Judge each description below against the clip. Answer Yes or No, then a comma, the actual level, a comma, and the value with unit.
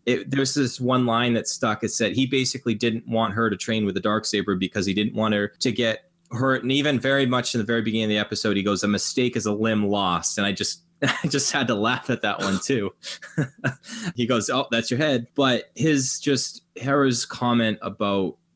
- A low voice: Yes, low, 120 Hz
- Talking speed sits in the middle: No, fast, 225 wpm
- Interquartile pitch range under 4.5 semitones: Yes, average, 4.1 semitones